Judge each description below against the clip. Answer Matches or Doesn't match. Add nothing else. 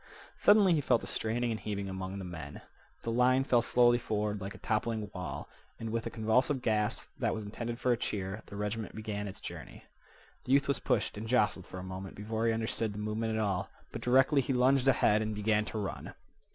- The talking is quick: Matches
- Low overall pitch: Matches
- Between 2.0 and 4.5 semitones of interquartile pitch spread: Matches